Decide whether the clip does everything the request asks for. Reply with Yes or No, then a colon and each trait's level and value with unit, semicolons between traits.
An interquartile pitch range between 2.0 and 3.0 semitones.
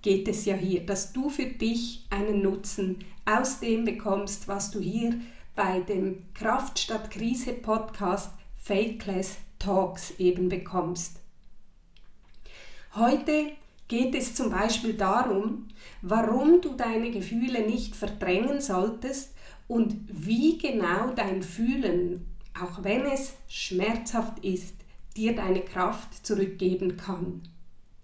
No: average, 3.7 semitones